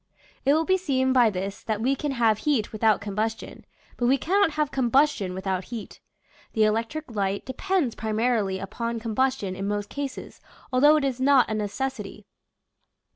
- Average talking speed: Yes, average, 165 wpm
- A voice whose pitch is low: No, high, 235 Hz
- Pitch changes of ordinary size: Yes, average, 4.6 semitones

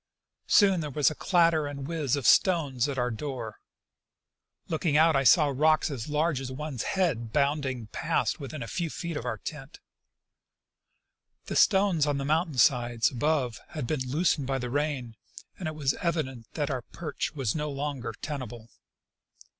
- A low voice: No, medium, 145 Hz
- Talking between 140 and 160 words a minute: No, average, 170 wpm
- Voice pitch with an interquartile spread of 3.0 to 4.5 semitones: Yes, average, 3.6 semitones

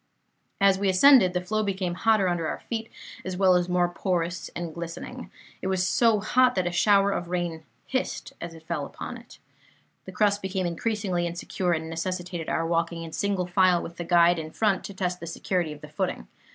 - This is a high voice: No, medium, 180 Hz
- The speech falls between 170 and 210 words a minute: Yes, fast, 205 wpm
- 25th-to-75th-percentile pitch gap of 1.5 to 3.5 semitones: Yes, narrow, 2.5 semitones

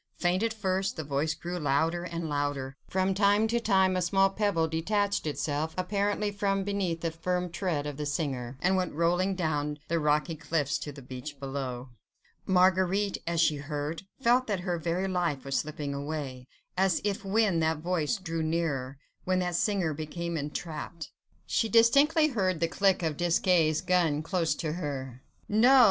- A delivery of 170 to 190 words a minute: Yes, average, 175 wpm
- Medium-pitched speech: Yes, medium, 170 Hz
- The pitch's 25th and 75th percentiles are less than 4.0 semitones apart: No, average, 4.3 semitones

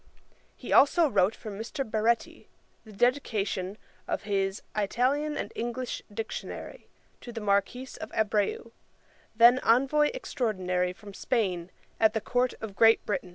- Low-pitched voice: No, high, 220 Hz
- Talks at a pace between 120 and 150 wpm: Yes, slow, 135 wpm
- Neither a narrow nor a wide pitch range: Yes, average, 3.8 semitones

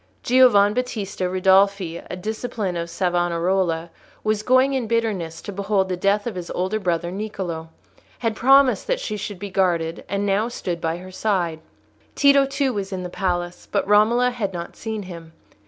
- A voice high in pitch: Yes, high, 195 Hz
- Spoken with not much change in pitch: No, average, 3.8 semitones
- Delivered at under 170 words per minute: No, average, 175 wpm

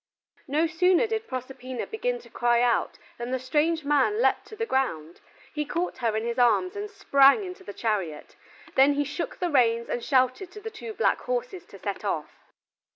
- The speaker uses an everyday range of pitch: No, wide, 7.5 semitones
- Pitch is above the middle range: Yes, very high, 285 Hz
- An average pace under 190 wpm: No, average, 195 wpm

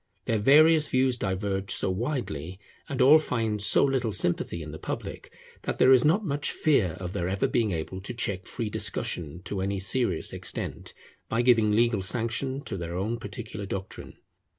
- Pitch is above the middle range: No, low, 110 Hz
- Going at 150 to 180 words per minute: Yes, average, 175 wpm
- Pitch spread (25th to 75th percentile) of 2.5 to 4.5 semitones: No, average, 5.3 semitones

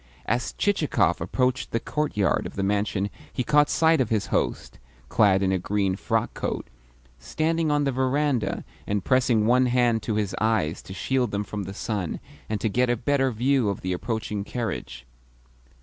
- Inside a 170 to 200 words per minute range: Yes, average, 180 wpm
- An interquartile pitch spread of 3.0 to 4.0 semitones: No, average, 4.4 semitones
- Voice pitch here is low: Yes, low, 110 Hz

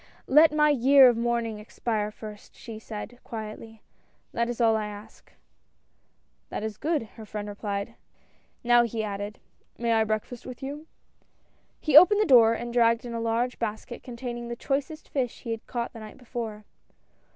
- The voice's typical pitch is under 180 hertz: No, high, 235 Hz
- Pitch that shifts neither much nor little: No, narrow, 2.3 semitones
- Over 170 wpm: Yes, average, 180 wpm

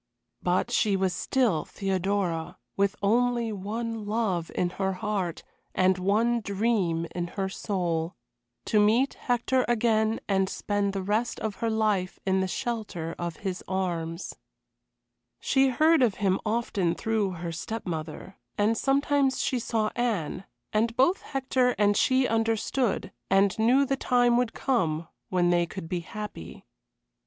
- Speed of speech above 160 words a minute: No, average, 145 wpm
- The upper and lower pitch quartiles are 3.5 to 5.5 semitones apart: Yes, average, 4.2 semitones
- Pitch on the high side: Yes, high, 205 Hz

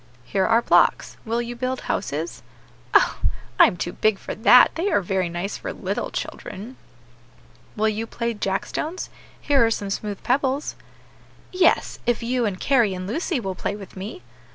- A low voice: No, high, 220 Hz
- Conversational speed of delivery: Yes, average, 175 wpm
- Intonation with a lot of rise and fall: No, average, 4.5 semitones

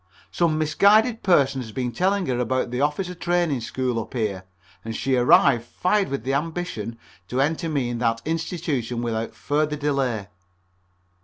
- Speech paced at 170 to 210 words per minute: No, average, 160 wpm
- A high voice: No, low, 135 Hz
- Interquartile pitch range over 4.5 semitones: Yes, wide, 5.5 semitones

